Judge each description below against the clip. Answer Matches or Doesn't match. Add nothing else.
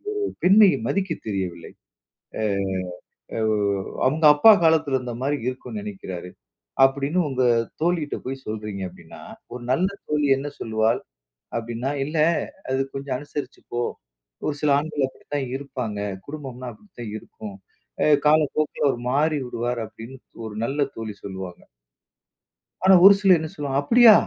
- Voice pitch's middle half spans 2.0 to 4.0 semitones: Doesn't match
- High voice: Doesn't match